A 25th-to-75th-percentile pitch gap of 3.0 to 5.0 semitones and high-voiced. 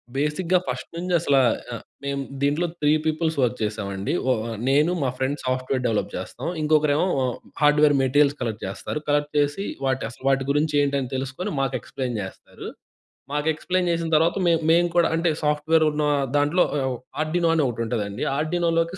No: average, 3.7 semitones; medium, 150 Hz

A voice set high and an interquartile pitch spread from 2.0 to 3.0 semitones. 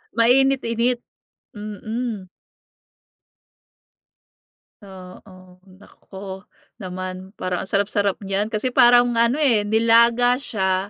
No: high, 210 Hz; average, 3.9 semitones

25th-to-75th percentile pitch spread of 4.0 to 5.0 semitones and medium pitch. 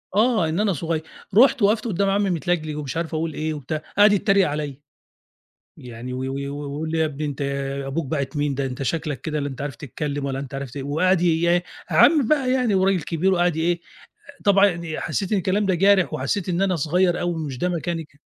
Yes: average, 4.7 semitones; medium, 165 Hz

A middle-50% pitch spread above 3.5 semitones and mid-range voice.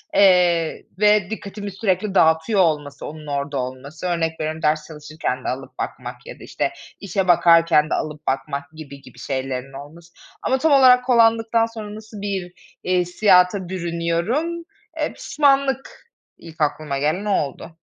Yes: wide, 5.5 semitones; medium, 170 Hz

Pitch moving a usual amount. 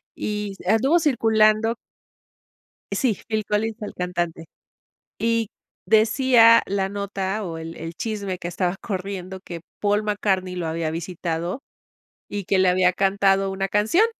Yes: average, 3.2 semitones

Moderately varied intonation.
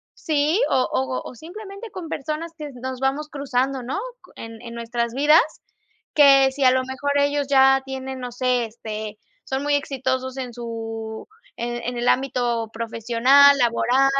Yes: average, 3.1 semitones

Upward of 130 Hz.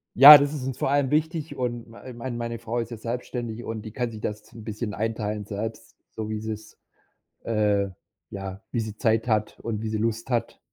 No: low, 115 Hz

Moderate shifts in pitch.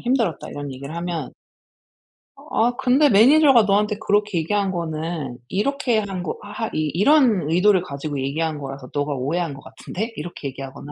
No: wide, 6.4 semitones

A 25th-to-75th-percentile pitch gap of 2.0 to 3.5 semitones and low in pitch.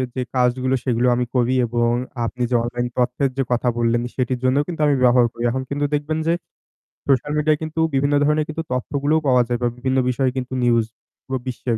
Yes: narrow, 2.6 semitones; low, 130 Hz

